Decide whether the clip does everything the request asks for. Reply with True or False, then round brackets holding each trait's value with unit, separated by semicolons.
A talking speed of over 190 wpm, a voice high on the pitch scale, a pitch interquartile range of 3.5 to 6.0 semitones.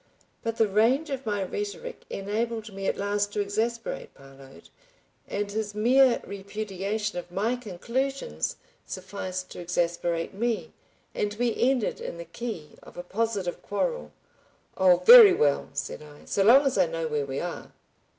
False (155 wpm; 205 Hz; 4.6 semitones)